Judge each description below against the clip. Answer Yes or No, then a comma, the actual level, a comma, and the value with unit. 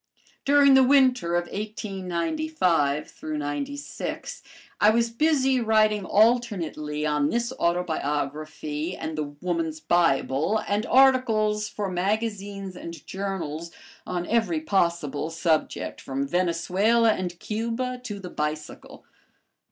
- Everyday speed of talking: No, slow, 105 wpm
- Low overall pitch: No, medium, 185 Hz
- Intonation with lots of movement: Yes, wide, 6.2 semitones